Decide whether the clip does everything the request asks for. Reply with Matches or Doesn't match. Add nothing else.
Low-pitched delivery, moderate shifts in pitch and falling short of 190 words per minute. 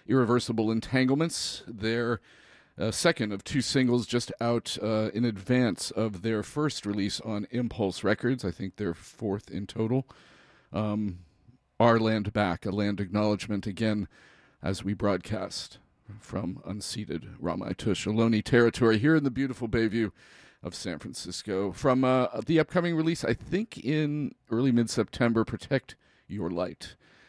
Matches